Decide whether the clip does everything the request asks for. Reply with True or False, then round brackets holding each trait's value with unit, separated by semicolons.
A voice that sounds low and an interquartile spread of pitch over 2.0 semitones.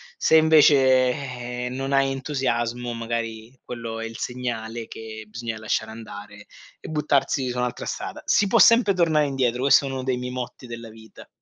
True (125 Hz; 2.9 semitones)